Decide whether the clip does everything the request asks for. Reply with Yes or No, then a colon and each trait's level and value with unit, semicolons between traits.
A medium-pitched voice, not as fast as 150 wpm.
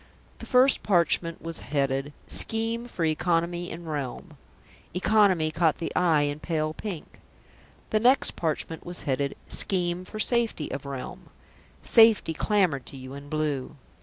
Yes: medium, 165 Hz; average, 140 wpm